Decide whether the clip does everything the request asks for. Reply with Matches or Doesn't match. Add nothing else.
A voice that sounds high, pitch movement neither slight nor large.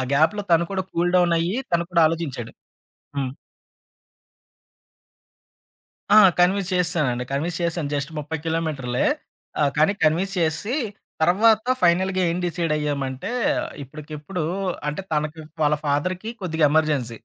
Doesn't match